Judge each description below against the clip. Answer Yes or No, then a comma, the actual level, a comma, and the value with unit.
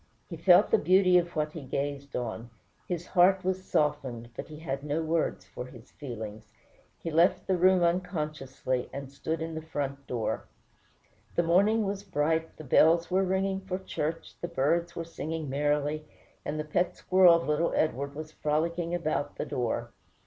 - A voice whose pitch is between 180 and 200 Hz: No, medium, 160 Hz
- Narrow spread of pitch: No, average, 3.8 semitones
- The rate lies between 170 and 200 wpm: Yes, average, 175 wpm